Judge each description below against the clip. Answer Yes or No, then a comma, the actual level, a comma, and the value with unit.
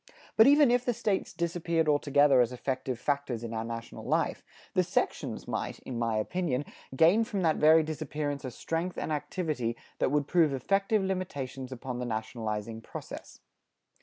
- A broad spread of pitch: Yes, wide, 5.7 semitones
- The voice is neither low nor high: Yes, medium, 145 Hz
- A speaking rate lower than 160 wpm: No, average, 165 wpm